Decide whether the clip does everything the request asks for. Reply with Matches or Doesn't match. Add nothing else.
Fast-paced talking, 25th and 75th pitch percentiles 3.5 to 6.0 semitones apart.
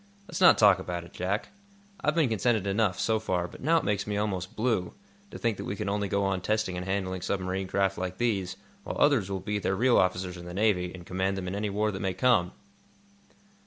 Doesn't match